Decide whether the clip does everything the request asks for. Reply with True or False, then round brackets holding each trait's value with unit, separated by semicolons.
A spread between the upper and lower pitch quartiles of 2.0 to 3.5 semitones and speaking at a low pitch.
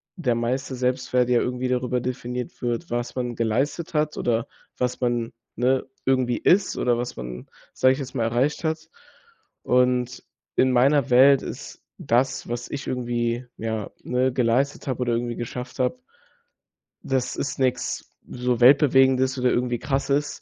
False (1.6 semitones; 125 Hz)